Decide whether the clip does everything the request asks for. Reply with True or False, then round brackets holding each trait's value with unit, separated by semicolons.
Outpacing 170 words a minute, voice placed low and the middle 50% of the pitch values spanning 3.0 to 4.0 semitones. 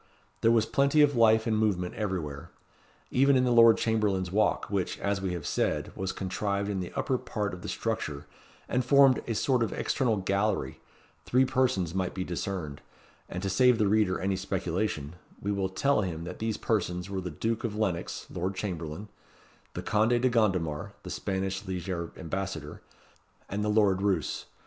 True (180 wpm; 100 Hz; 3.5 semitones)